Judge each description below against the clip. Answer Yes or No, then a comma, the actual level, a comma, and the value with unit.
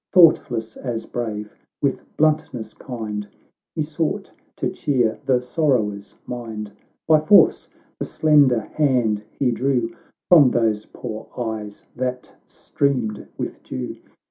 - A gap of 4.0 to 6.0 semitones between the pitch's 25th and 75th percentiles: Yes, average, 4.3 semitones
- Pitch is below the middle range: Yes, low, 120 Hz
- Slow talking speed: Yes, slow, 115 wpm